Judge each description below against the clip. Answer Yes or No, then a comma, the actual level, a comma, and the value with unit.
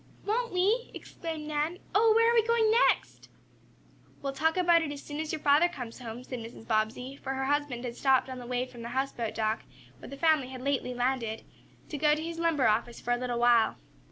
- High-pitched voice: Yes, very high, 275 Hz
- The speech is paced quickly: Yes, fast, 220 wpm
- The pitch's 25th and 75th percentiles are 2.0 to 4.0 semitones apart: No, average, 5.1 semitones